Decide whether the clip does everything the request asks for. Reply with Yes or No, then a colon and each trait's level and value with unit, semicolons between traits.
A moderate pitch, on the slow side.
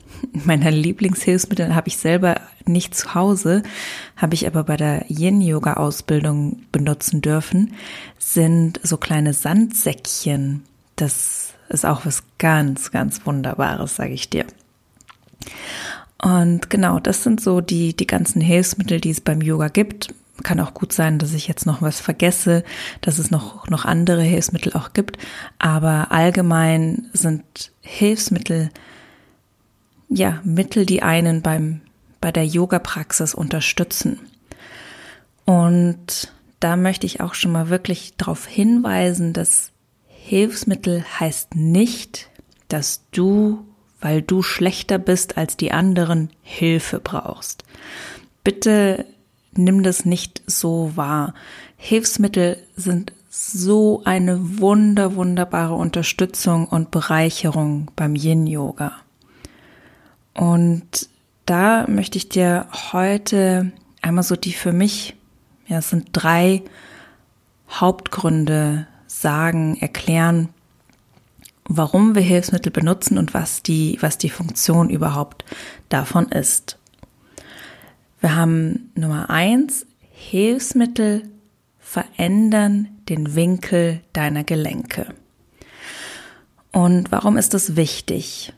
Yes: medium, 175 Hz; slow, 110 wpm